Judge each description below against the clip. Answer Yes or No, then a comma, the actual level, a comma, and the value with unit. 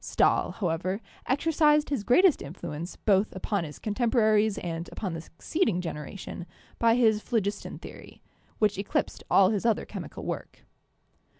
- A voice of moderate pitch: No, high, 210 Hz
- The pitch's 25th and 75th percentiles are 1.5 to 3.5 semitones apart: No, average, 4.3 semitones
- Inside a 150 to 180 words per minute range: No, slow, 135 wpm